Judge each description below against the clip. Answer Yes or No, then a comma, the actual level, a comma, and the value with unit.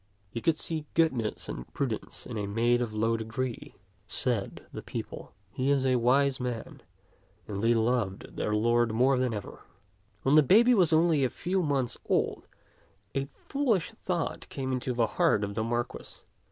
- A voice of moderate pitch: No, low, 125 Hz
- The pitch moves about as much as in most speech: Yes, average, 3.9 semitones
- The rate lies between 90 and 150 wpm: No, average, 180 wpm